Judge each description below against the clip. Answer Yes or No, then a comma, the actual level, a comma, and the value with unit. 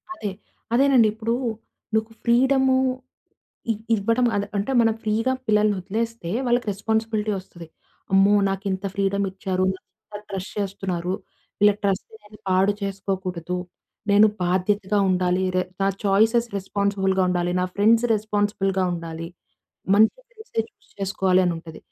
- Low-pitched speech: No, high, 200 Hz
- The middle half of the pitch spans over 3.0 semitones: No, average, 2.7 semitones